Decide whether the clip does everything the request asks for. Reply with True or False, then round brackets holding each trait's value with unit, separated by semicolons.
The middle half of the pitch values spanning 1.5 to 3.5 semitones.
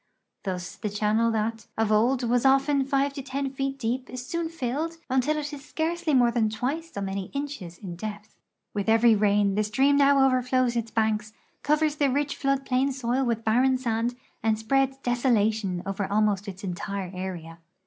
False (4.4 semitones)